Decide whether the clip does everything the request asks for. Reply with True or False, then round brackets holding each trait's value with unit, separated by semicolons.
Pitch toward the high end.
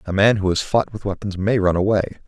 False (100 Hz)